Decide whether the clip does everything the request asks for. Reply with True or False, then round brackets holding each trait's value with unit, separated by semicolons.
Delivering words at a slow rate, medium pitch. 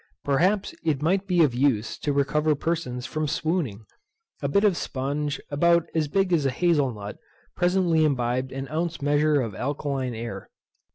False (165 wpm; 145 Hz)